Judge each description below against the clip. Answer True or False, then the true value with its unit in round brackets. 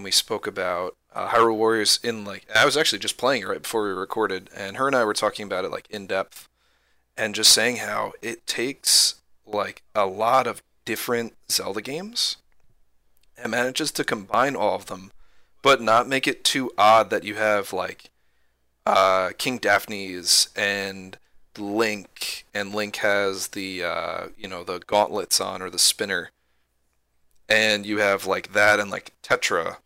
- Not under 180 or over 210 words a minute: False (170 wpm)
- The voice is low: True (100 Hz)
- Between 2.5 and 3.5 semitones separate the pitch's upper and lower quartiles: True (3.1 semitones)